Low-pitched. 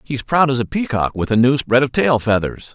Yes: low, 125 Hz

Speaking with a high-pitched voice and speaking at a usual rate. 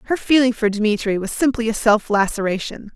Yes: high, 225 Hz; average, 185 wpm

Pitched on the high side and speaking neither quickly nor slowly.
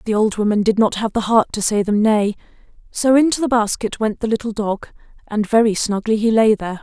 No: high, 215 Hz; fast, 230 wpm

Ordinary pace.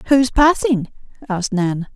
Yes: average, 155 wpm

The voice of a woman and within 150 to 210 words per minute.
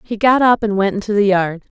No: female; fast, 270 wpm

